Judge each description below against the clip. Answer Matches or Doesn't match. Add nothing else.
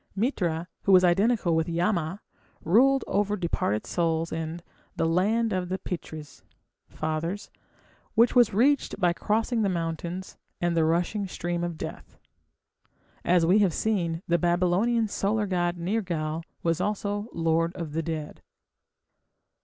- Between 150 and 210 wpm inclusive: Doesn't match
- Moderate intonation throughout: Matches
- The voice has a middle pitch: Matches